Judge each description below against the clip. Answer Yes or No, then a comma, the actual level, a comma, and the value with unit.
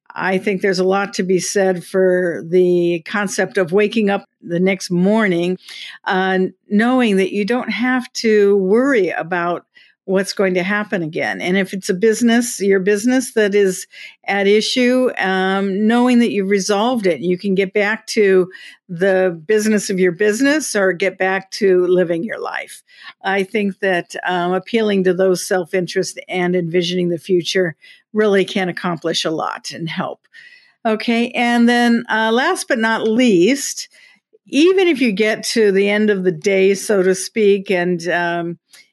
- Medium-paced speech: Yes, average, 165 wpm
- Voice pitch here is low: No, high, 195 Hz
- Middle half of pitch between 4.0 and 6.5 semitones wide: No, average, 3.0 semitones